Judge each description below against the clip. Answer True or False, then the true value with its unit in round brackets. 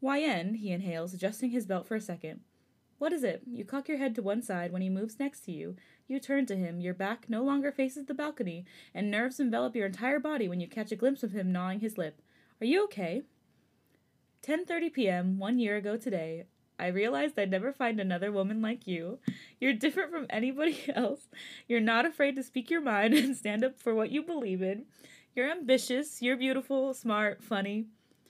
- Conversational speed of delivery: False (210 wpm)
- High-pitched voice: True (235 Hz)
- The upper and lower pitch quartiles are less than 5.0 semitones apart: False (5.6 semitones)